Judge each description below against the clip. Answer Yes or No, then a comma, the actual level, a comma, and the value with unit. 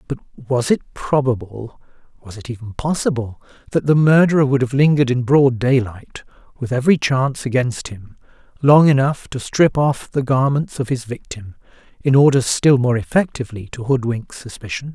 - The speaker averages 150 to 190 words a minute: Yes, average, 155 wpm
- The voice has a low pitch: Yes, low, 130 Hz